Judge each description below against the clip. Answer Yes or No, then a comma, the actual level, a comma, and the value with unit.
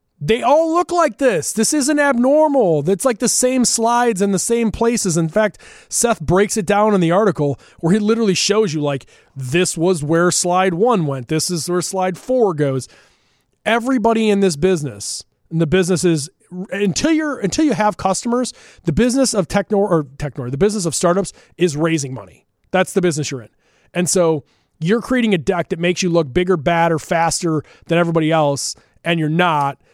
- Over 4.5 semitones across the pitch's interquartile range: Yes, average, 5.1 semitones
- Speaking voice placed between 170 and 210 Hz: Yes, medium, 185 Hz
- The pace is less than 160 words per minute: No, average, 190 wpm